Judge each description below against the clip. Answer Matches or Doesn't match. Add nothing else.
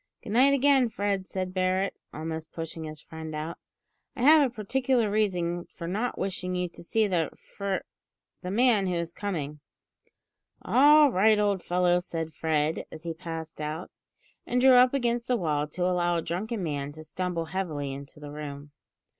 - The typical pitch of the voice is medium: Matches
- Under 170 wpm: Doesn't match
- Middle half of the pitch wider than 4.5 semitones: Matches